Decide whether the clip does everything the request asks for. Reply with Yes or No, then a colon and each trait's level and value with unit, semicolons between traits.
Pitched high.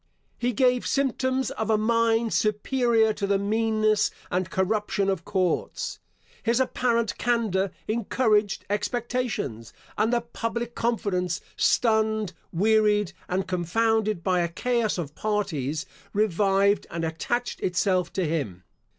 Yes: high, 215 Hz